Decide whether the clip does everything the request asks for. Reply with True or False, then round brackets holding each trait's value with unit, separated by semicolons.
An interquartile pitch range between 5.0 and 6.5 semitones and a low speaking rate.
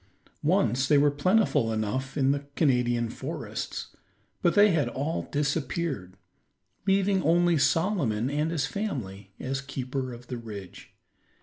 True (5.4 semitones; 130 wpm)